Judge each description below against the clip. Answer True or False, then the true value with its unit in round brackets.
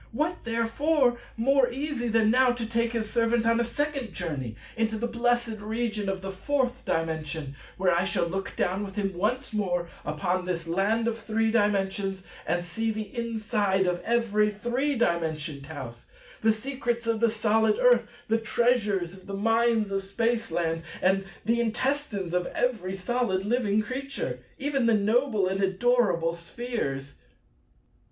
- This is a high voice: True (220 Hz)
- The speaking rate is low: False (155 wpm)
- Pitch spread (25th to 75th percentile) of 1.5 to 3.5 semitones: False (4.0 semitones)